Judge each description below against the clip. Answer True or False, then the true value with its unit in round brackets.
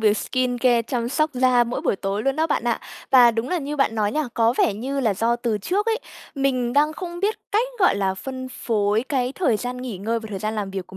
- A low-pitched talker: False (245 Hz)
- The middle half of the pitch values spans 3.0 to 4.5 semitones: True (4.0 semitones)